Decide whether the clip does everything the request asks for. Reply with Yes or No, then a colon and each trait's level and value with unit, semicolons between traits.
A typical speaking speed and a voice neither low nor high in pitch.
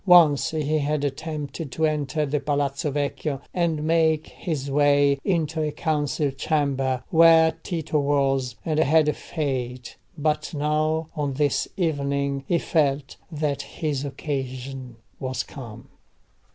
No: slow, 125 wpm; medium, 145 Hz